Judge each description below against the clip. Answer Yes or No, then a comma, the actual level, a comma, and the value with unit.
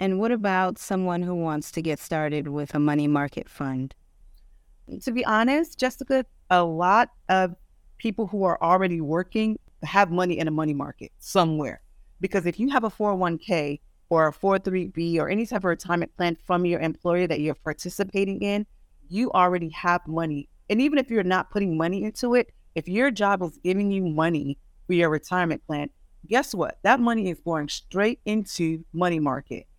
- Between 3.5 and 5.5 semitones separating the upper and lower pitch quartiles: Yes, average, 4.4 semitones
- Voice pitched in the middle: Yes, medium, 180 Hz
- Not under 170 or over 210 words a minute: Yes, average, 180 wpm